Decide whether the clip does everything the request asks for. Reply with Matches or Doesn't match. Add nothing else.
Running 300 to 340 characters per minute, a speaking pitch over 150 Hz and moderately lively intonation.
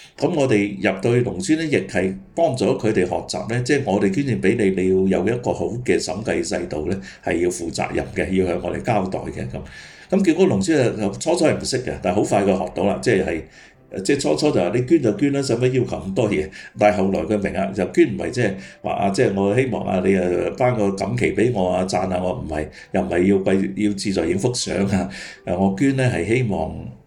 Doesn't match